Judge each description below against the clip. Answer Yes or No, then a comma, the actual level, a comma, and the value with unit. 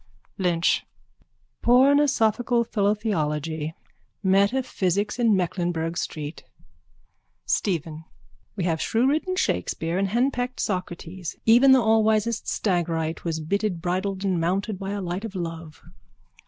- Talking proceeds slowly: Yes, slow, 105 wpm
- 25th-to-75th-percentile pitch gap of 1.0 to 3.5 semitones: No, average, 4.9 semitones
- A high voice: Yes, high, 195 Hz